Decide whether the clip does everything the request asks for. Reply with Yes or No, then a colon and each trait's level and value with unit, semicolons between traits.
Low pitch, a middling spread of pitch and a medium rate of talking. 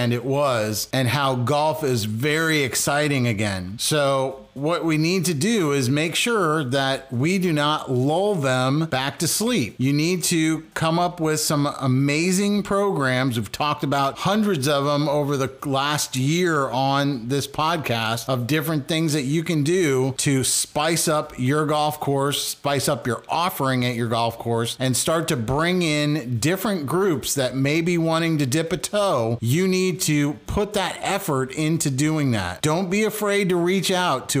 No: medium, 150 Hz; average, 3.8 semitones; average, 175 wpm